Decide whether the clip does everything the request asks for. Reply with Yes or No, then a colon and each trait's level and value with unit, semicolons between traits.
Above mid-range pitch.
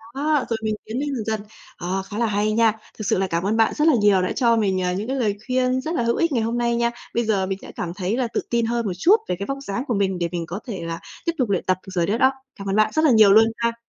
Yes: high, 220 Hz